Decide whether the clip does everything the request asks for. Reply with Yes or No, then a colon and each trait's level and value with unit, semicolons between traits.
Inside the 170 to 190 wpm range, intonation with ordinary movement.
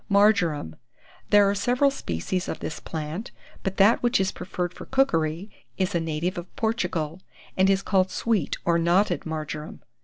No: average, 160 wpm; average, 3.9 semitones